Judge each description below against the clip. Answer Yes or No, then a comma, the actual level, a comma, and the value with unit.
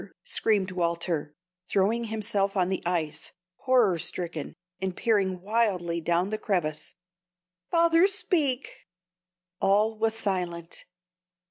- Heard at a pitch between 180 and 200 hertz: Yes, high, 190 Hz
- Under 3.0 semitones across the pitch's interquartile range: No, average, 4.4 semitones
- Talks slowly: Yes, slow, 105 wpm